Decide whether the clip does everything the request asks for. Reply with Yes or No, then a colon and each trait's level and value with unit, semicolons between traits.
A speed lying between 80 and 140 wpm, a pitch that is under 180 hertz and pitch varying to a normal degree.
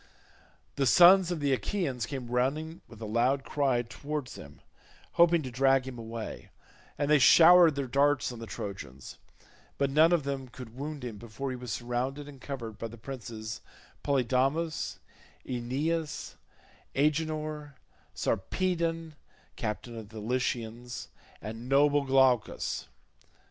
Yes: slow, 135 wpm; low, 135 Hz; average, 4.0 semitones